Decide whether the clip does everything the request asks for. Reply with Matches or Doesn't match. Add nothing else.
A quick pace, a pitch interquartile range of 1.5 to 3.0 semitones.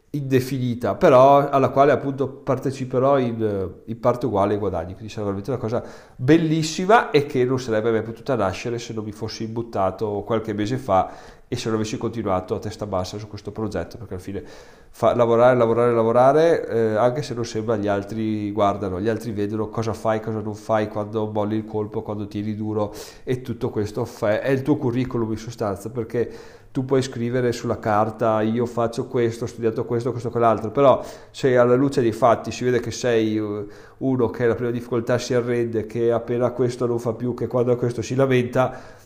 Matches